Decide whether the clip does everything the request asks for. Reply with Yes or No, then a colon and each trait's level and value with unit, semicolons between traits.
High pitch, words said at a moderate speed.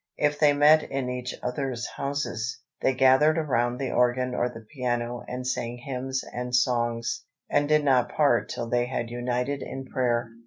No: low, 125 Hz; average, 170 wpm